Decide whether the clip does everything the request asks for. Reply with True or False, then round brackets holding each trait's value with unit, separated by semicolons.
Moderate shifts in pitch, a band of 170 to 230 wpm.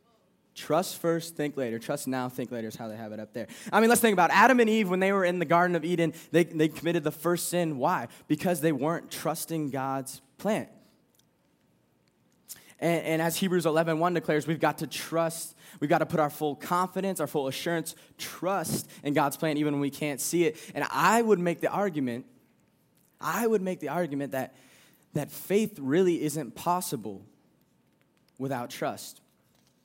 True (3.4 semitones; 190 wpm)